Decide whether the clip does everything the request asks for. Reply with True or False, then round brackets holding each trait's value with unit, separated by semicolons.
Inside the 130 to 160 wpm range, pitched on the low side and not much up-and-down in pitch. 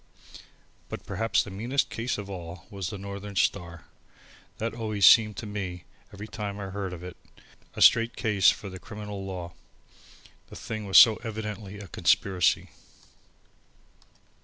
True (150 wpm; 100 Hz; 2.2 semitones)